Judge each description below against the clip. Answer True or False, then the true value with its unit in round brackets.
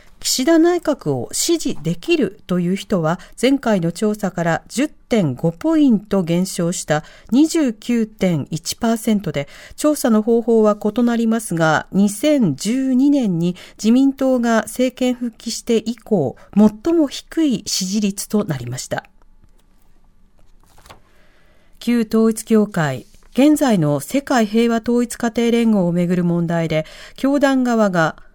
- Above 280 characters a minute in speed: False (210 characters per minute)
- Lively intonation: True (5.9 semitones)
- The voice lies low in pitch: False (220 Hz)